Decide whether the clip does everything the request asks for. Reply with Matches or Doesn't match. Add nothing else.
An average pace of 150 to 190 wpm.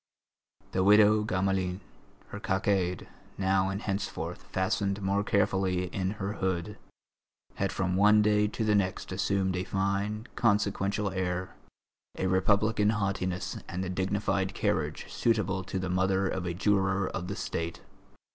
Doesn't match